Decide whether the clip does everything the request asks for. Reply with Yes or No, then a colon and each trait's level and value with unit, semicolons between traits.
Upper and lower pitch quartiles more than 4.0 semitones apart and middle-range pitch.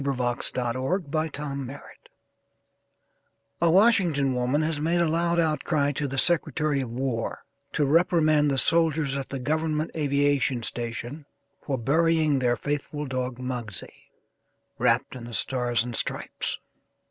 No: average, 3.6 semitones; medium, 145 Hz